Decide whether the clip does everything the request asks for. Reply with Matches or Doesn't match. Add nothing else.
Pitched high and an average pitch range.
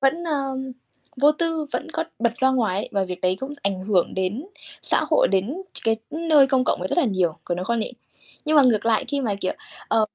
Doesn't match